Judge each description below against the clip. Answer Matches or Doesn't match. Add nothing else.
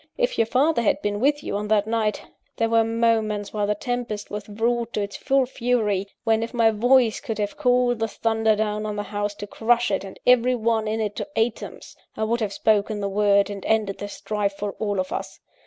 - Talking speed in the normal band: Doesn't match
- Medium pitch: Doesn't match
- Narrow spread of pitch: Matches